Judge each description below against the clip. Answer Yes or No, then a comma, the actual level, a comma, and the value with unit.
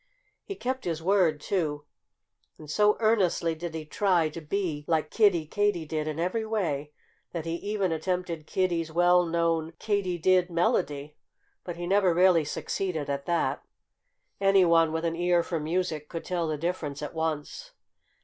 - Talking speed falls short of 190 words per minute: Yes, average, 160 wpm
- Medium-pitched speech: Yes, medium, 170 Hz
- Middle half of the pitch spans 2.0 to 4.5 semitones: Yes, average, 2.8 semitones